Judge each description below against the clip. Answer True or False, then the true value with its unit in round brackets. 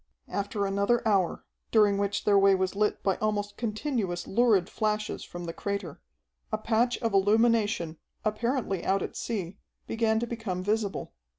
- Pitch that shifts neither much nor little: False (2.3 semitones)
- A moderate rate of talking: True (155 wpm)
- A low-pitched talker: False (205 Hz)